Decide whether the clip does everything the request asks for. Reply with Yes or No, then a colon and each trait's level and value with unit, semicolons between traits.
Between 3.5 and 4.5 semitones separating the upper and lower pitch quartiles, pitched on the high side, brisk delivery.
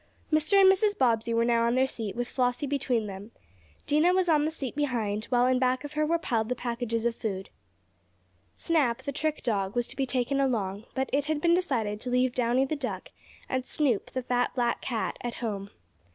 Yes: average, 3.8 semitones; very high, 250 Hz; fast, 210 wpm